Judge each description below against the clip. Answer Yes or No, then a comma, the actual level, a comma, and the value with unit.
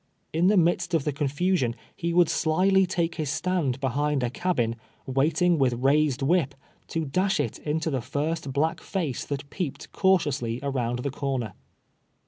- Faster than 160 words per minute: Yes, average, 170 wpm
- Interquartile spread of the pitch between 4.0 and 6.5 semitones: Yes, average, 4.3 semitones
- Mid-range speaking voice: Yes, medium, 150 Hz